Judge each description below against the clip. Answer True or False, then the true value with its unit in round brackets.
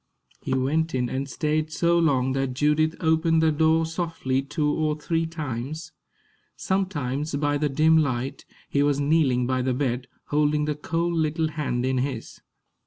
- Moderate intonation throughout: True (3.2 semitones)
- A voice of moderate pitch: True (150 Hz)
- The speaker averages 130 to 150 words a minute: False (165 wpm)